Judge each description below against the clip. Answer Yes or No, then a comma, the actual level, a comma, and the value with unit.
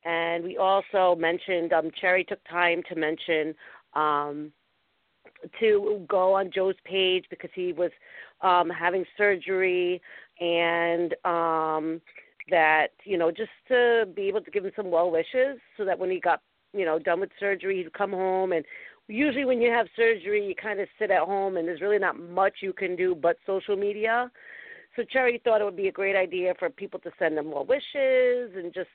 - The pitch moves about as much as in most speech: Yes, average, 3.7 semitones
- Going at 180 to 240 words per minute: Yes, average, 190 wpm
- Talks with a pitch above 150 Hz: Yes, medium, 185 Hz